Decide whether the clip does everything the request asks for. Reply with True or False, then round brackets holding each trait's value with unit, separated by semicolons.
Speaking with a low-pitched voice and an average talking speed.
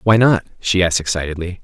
True (95 Hz; 185 wpm)